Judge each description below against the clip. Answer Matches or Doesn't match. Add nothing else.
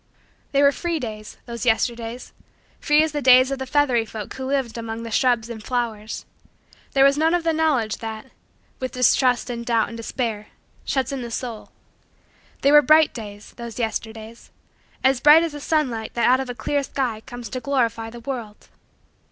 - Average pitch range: Matches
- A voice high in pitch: Matches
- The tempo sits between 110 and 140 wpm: Doesn't match